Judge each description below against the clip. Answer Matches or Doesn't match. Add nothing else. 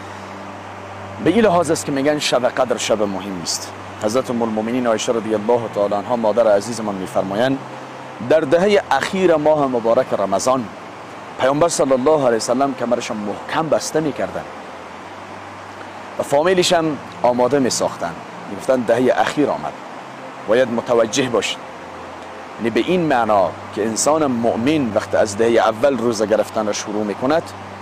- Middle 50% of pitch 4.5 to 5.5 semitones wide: Matches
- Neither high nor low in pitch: Doesn't match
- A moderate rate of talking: Matches